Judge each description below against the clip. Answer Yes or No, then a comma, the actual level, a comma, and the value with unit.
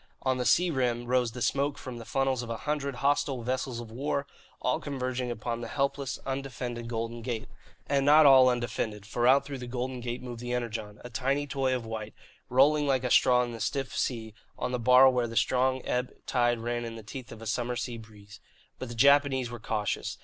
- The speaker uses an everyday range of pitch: No, narrow, 2.3 semitones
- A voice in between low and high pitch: No, low, 125 Hz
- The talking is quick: Yes, fast, 215 wpm